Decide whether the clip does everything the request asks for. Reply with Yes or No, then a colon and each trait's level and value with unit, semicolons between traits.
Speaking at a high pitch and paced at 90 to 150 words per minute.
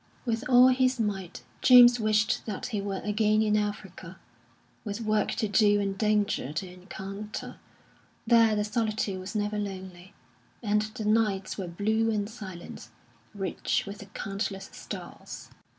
Yes: high, 210 Hz; average, 145 wpm